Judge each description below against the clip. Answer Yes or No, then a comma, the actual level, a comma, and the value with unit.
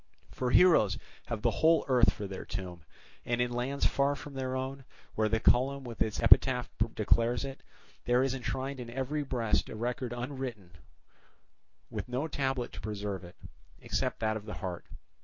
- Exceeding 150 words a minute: Yes, average, 175 wpm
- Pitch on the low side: Yes, low, 125 Hz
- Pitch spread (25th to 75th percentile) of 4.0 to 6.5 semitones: No, average, 3.6 semitones